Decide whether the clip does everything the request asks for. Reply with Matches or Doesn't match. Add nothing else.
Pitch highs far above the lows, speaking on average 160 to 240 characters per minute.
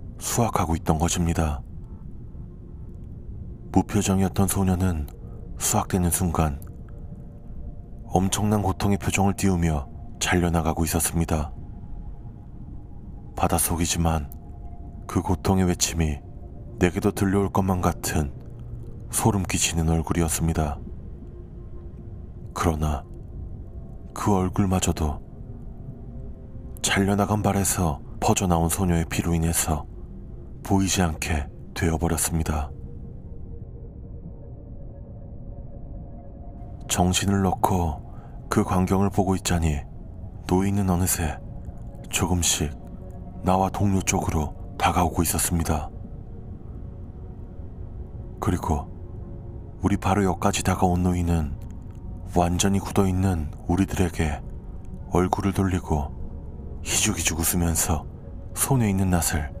Doesn't match